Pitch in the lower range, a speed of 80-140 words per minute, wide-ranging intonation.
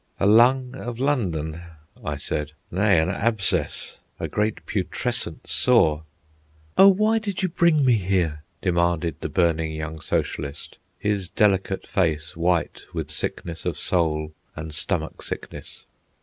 Yes: very low, 90 Hz; slow, 135 wpm; wide, 6.7 semitones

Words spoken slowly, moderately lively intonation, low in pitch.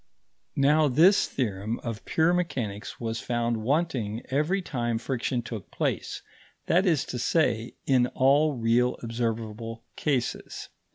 Yes: slow, 125 wpm; average, 4.6 semitones; low, 125 Hz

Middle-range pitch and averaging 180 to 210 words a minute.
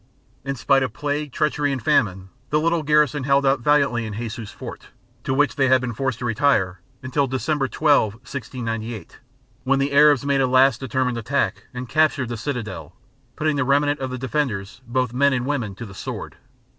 No: low, 130 Hz; average, 190 wpm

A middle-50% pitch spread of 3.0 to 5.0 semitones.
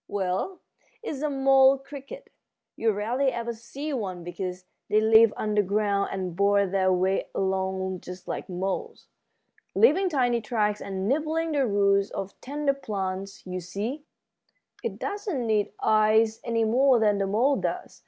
No: wide, 5.6 semitones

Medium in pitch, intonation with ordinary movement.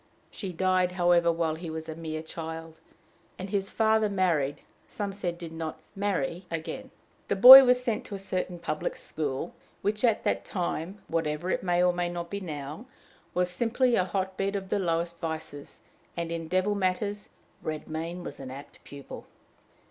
Yes: medium, 175 Hz; average, 3.3 semitones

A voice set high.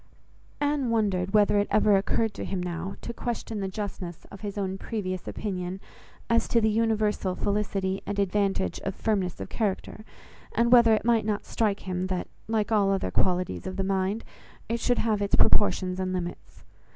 Yes: high, 200 Hz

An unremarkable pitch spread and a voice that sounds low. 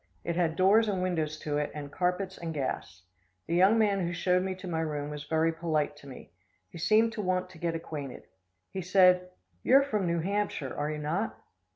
No: average, 3.6 semitones; medium, 170 Hz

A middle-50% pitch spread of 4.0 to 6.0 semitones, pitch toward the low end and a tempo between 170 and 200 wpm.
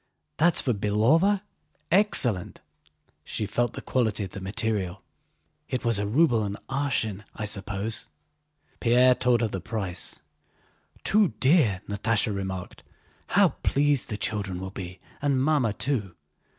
No: average, 4.7 semitones; low, 110 Hz; slow, 135 wpm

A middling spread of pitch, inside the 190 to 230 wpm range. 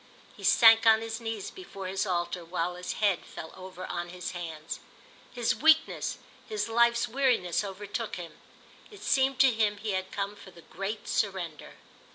No: average, 4.1 semitones; average, 170 wpm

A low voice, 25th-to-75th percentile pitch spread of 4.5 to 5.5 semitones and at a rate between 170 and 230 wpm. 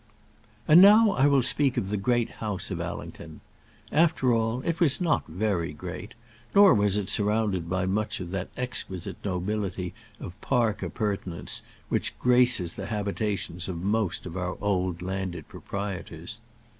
No: low, 100 Hz; average, 4.9 semitones; average, 150 wpm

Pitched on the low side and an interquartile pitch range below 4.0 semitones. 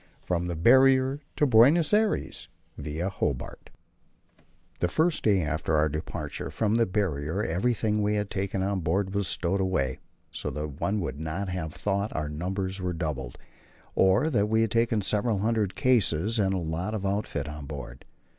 No: very low, 95 Hz; average, 5.2 semitones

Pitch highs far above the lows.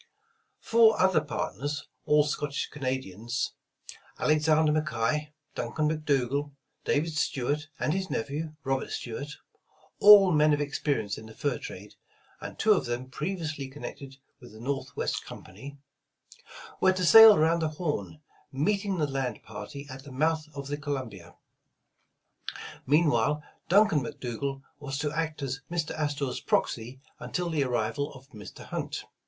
No: average, 2.9 semitones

